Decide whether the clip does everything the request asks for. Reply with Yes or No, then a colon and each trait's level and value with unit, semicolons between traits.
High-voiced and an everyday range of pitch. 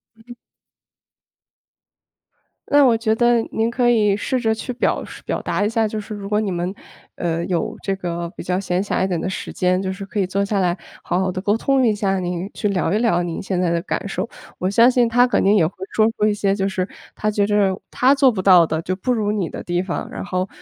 Yes: high, 200 Hz; average, 3.3 semitones